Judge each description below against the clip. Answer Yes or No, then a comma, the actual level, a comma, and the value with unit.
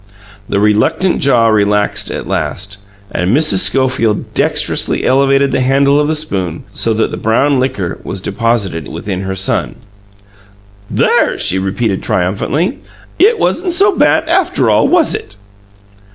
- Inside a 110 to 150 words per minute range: Yes, average, 140 wpm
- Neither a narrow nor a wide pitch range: No, wide, 6.9 semitones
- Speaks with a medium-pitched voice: No, low, 115 Hz